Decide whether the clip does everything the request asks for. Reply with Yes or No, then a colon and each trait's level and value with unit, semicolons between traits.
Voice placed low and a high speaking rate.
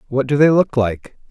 Yes: low, 130 Hz; fast, 230 wpm